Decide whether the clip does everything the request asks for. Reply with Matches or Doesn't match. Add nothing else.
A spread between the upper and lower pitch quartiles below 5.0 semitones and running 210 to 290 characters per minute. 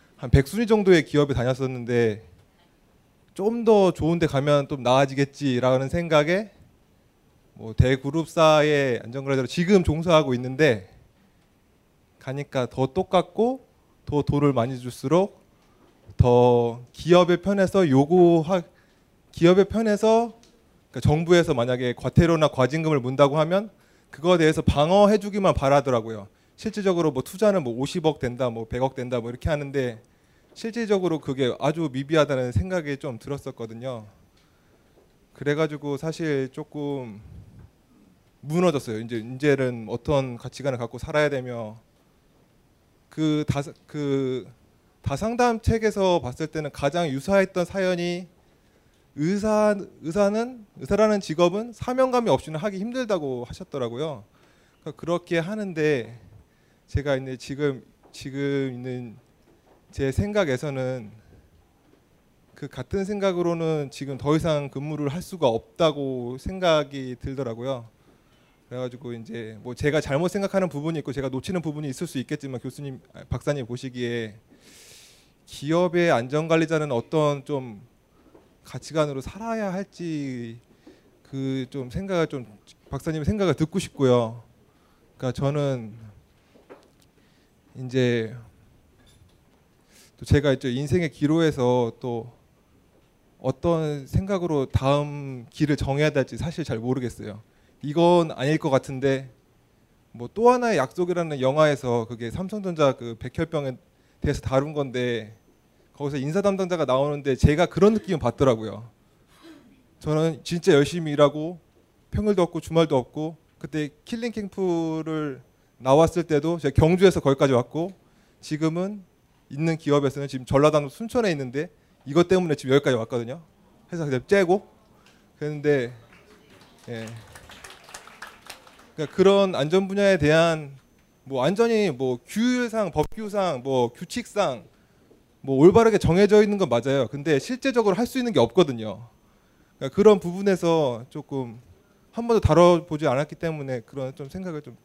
Doesn't match